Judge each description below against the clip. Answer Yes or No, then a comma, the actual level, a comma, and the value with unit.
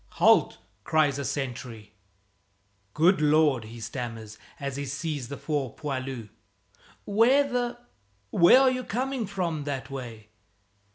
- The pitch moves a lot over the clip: Yes, wide, 6.6 semitones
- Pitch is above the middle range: No, medium, 145 Hz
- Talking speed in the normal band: No, slow, 125 wpm